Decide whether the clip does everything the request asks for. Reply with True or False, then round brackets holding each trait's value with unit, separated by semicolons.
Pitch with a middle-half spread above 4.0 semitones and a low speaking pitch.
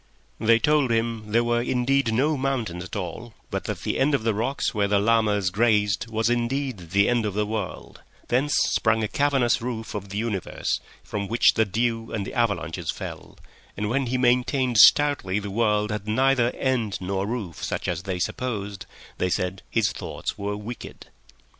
False (3.2 semitones; 110 Hz)